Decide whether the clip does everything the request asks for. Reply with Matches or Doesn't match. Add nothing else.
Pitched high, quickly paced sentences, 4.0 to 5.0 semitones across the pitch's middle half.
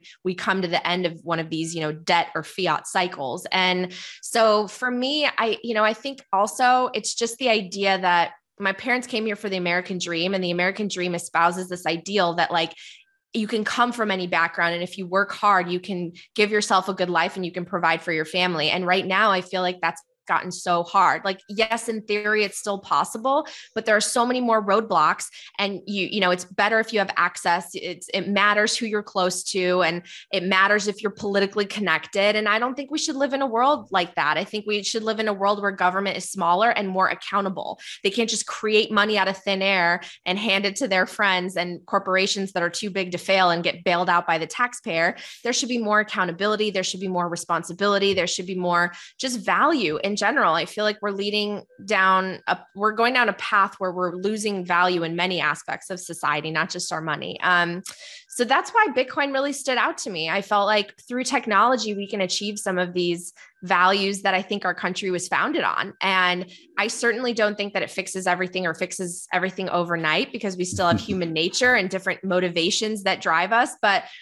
Doesn't match